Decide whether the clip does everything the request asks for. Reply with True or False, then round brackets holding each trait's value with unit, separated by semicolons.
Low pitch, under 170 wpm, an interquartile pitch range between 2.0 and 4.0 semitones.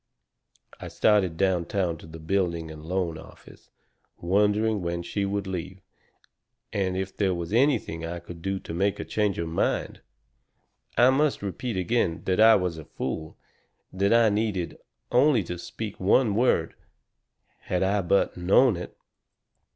True (95 Hz; 150 wpm; 3.5 semitones)